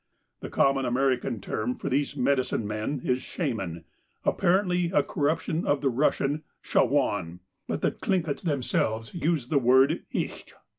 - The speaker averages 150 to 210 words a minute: No, average, 140 wpm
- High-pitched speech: No, low, 135 Hz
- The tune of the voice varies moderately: Yes, average, 3.7 semitones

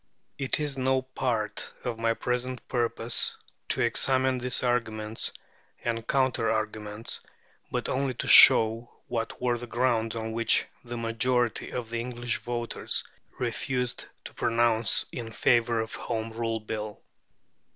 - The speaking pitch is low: Yes, low, 120 Hz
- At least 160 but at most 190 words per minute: No, average, 140 wpm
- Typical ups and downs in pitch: No, narrow, 1.9 semitones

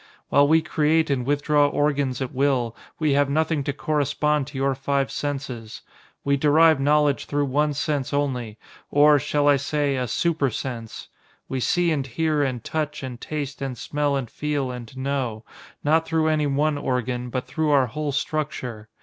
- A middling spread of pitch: No, narrow, 2.3 semitones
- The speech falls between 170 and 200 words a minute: Yes, average, 175 wpm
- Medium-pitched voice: Yes, medium, 145 Hz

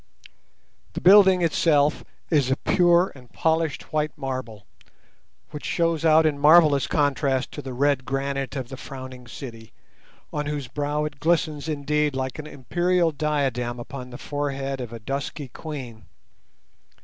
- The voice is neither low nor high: Yes, medium, 145 Hz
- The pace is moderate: Yes, average, 145 wpm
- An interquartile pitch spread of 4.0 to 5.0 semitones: No, average, 2.8 semitones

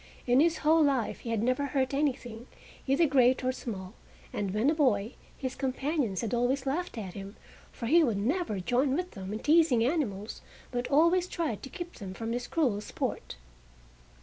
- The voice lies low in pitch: No, very high, 255 Hz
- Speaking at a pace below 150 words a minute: No, average, 185 wpm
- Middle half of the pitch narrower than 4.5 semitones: No, average, 4.9 semitones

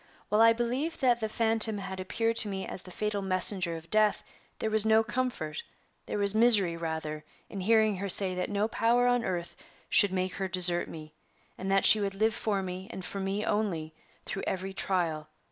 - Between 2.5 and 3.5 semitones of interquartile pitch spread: Yes, average, 3.1 semitones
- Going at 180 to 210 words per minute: Yes, average, 200 wpm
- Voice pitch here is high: Yes, high, 195 Hz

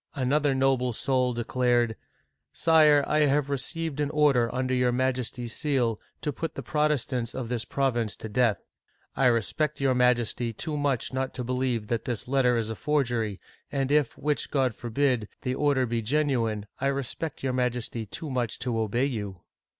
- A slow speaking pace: No, average, 175 wpm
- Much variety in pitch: No, average, 3.1 semitones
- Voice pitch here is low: Yes, low, 130 Hz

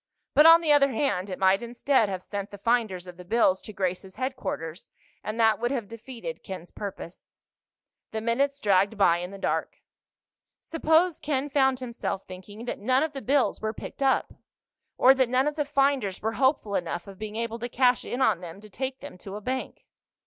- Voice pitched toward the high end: Yes, high, 230 Hz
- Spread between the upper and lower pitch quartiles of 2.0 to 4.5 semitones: No, wide, 5.4 semitones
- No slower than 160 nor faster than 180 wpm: No, average, 200 wpm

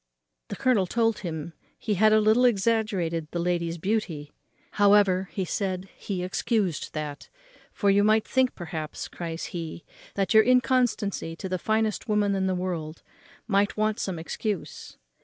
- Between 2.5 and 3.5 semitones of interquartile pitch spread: No, average, 4.0 semitones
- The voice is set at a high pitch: Yes, high, 195 Hz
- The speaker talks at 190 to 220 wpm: No, average, 155 wpm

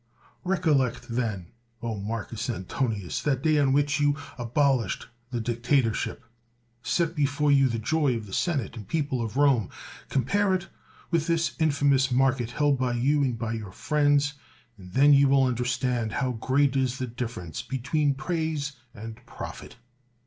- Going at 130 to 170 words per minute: Yes, average, 155 wpm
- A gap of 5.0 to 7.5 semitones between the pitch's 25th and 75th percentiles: No, average, 3.7 semitones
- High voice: No, low, 130 Hz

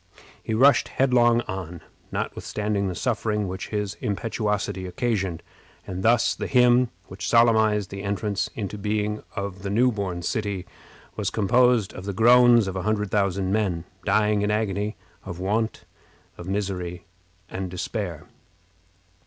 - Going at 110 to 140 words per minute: Yes, slow, 135 wpm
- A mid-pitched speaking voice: No, low, 105 Hz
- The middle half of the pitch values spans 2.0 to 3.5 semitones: Yes, average, 2.7 semitones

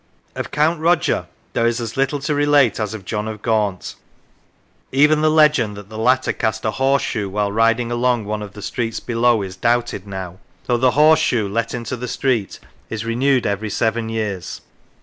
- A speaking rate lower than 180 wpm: No, average, 190 wpm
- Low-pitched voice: Yes, low, 115 Hz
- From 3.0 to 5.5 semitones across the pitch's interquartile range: Yes, average, 3.9 semitones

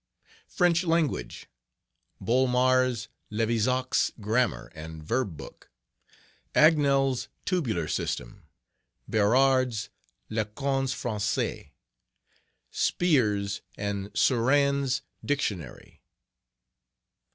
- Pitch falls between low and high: No, low, 125 Hz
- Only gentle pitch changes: No, average, 4.8 semitones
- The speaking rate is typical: No, slow, 60 wpm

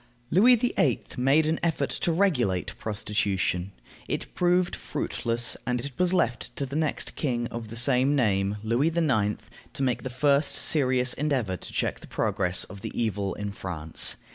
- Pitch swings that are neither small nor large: No, wide, 6.3 semitones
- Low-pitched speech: Yes, low, 125 Hz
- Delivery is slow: No, average, 165 wpm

